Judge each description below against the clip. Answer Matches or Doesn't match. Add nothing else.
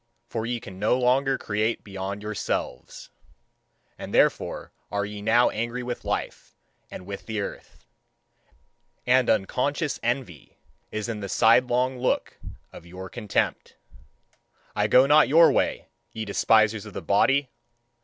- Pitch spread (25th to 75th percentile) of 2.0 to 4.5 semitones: Matches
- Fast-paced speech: Doesn't match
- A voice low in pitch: Matches